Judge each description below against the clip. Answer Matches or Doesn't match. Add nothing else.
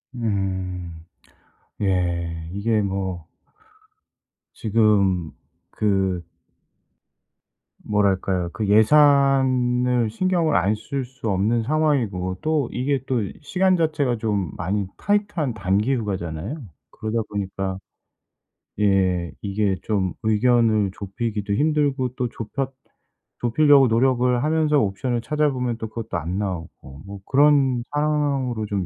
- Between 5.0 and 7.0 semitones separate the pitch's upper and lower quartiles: Matches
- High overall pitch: Doesn't match